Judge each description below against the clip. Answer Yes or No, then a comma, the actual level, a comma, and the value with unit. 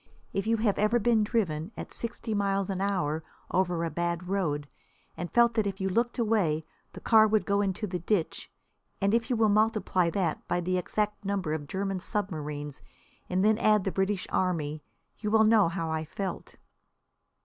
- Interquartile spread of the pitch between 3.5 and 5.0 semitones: Yes, average, 3.8 semitones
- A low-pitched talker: No, high, 195 Hz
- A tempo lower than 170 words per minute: No, average, 185 wpm